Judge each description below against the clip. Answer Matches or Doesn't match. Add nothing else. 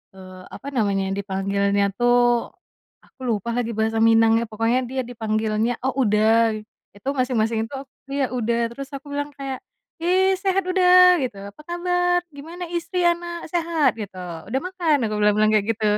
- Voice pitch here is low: Doesn't match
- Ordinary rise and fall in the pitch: Doesn't match